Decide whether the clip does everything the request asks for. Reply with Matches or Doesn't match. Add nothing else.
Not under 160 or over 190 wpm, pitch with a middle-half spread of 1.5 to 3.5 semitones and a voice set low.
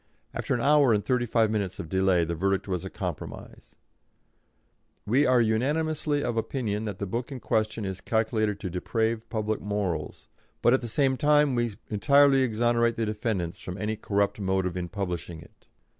Doesn't match